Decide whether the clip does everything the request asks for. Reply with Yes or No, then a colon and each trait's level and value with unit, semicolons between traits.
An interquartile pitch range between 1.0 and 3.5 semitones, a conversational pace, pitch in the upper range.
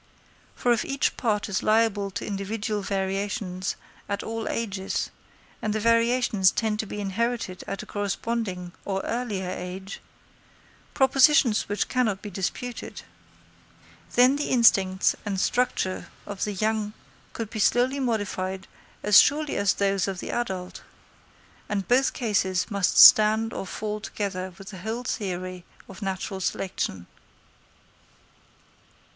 No: average, 3.2 semitones; slow, 130 wpm; high, 205 Hz